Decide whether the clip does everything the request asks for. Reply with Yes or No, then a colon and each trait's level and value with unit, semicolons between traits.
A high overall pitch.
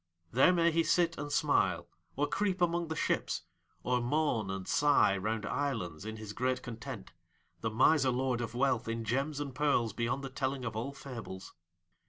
No: low, 130 Hz